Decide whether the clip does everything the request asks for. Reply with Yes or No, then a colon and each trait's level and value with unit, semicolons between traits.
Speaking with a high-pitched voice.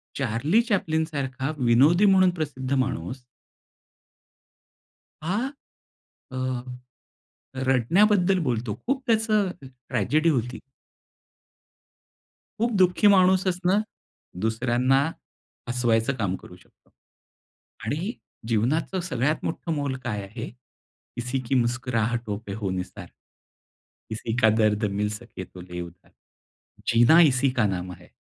No: low, 130 Hz